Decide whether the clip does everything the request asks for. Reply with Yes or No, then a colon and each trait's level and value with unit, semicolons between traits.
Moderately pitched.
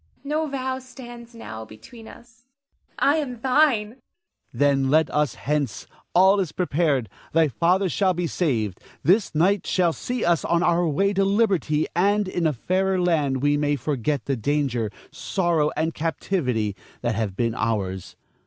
Yes: medium, 170 Hz